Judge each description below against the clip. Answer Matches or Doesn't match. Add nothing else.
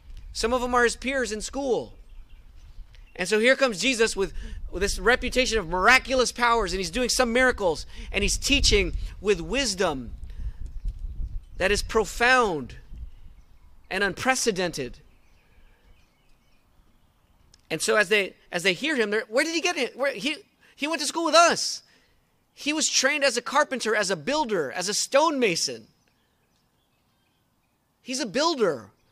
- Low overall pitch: Doesn't match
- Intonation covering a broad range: Matches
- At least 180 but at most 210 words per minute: Doesn't match